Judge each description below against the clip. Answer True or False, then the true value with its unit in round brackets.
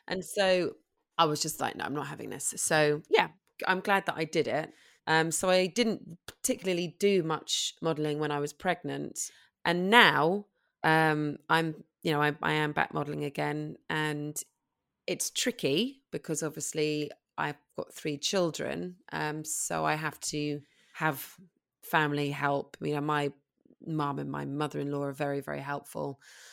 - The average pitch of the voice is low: False (155 Hz)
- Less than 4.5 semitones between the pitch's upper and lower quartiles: True (3.4 semitones)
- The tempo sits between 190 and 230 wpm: False (165 wpm)